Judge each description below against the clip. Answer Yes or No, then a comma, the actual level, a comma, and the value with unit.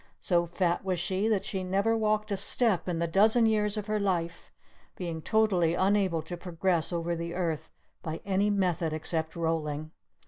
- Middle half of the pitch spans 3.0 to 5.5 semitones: Yes, average, 3.5 semitones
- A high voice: No, medium, 180 Hz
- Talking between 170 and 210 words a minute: Yes, average, 180 wpm